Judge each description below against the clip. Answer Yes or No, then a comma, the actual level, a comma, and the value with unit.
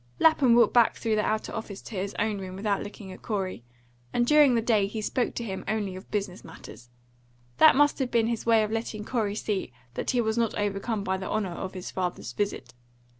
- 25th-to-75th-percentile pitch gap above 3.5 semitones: No, average, 3.1 semitones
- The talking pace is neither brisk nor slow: No, fast, 225 wpm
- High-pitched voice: Yes, high, 210 Hz